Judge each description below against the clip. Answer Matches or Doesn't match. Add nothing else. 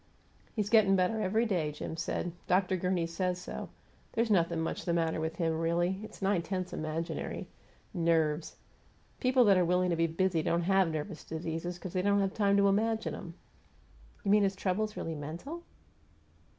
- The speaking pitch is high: Doesn't match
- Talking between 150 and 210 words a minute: Matches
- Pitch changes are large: Doesn't match